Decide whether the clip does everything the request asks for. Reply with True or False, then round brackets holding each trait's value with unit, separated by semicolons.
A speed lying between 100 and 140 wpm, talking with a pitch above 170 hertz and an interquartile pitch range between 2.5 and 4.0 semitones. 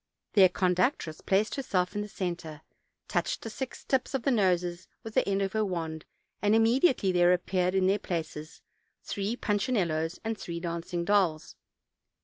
False (165 wpm; 185 Hz; 3.6 semitones)